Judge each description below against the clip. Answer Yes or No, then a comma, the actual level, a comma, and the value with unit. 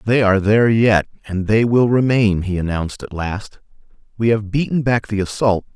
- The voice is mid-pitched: No, low, 105 Hz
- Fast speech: No, average, 190 wpm